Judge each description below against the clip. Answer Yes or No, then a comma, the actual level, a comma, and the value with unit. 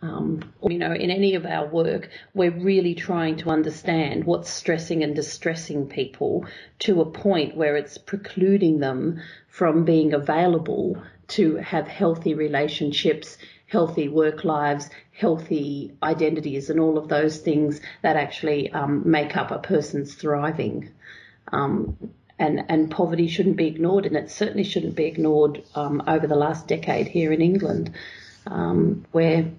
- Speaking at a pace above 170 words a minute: No, average, 150 wpm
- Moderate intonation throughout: No, narrow, 2.2 semitones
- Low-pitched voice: No, medium, 160 Hz